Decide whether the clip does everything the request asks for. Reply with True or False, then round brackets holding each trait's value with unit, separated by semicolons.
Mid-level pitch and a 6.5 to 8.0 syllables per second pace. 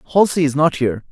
True (145 Hz; 7.7 syllables/s)